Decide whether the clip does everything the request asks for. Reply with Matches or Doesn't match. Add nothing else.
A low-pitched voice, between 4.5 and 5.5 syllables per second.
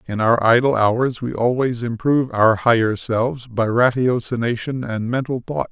Matches